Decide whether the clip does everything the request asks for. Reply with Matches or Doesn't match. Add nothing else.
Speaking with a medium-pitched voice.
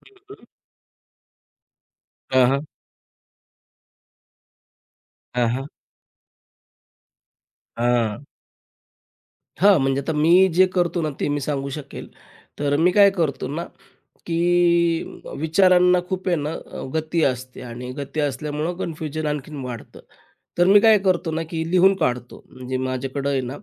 Matches